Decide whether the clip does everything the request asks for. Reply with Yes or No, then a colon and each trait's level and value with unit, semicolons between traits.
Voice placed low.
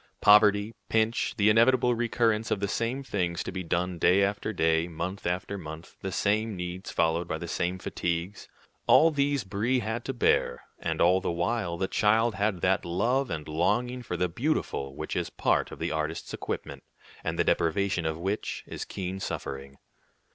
Yes: very low, 95 Hz